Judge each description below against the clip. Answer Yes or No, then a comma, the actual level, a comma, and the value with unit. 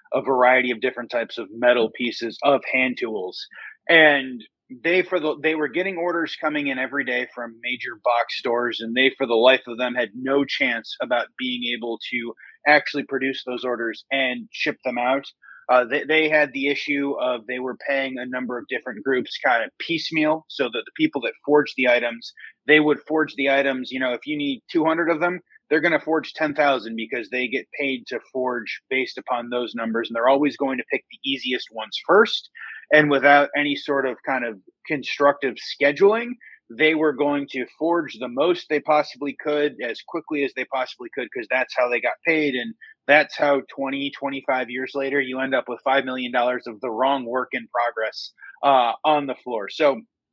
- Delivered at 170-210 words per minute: Yes, average, 200 wpm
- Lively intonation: No, average, 3.3 semitones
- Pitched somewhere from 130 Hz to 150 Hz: Yes, low, 135 Hz